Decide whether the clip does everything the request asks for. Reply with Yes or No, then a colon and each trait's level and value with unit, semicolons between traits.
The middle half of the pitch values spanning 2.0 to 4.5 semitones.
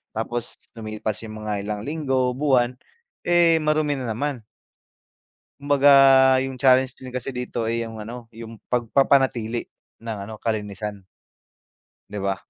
Yes: average, 3.5 semitones